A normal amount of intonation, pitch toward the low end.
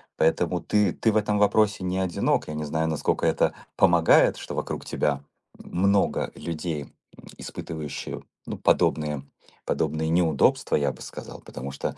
Yes: average, 3.7 semitones; very low, 80 Hz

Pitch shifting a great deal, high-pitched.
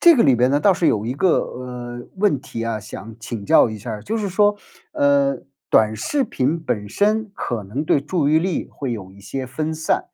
No: wide, 6.9 semitones; low, 135 Hz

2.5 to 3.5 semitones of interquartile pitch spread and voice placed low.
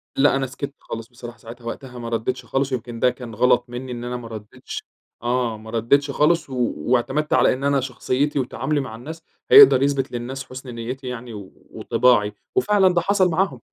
Yes: average, 2.9 semitones; low, 125 Hz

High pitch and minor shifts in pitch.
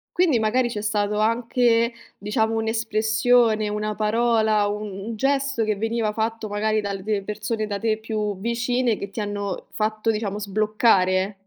Yes: high, 215 Hz; narrow, 1.6 semitones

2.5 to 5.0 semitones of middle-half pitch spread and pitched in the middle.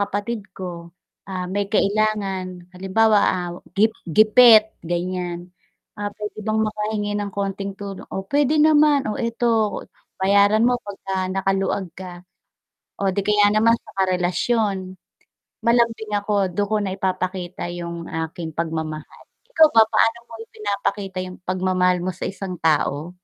No: average, 2.9 semitones; high, 195 Hz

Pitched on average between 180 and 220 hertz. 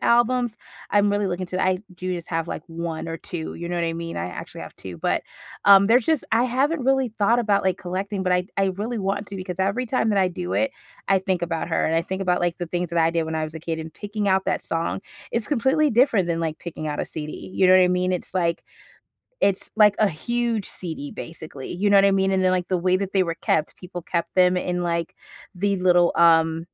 Yes: medium, 185 Hz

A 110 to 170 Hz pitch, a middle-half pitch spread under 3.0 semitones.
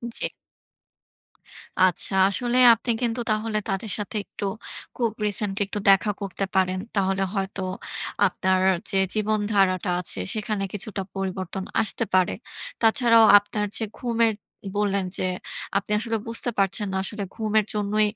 No: high, 205 Hz; narrow, 2.4 semitones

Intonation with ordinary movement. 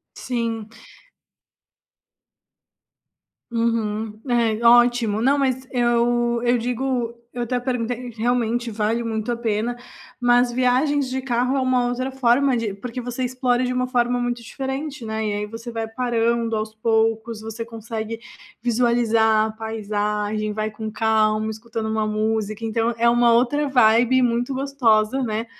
No: narrow, 2.0 semitones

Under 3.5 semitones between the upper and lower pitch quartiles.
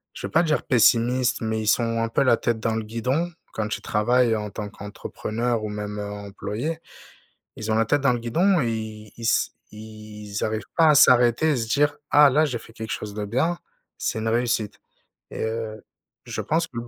Yes: average, 3.0 semitones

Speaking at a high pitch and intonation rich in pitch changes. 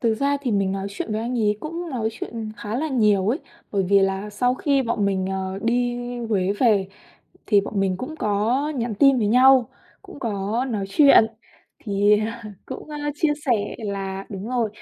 No: high, 220 Hz; average, 4.2 semitones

